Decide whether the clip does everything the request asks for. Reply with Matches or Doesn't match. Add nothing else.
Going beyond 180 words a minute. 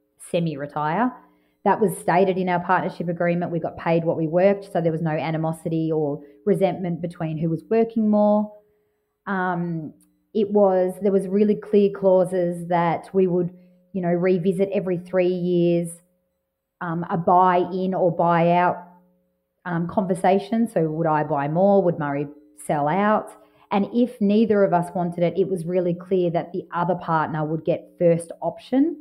Doesn't match